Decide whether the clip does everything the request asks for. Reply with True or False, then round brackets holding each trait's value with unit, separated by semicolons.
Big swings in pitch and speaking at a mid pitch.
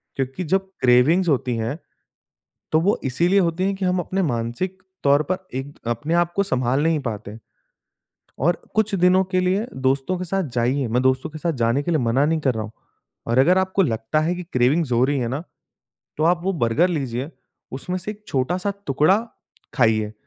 True (6.3 semitones; 150 Hz)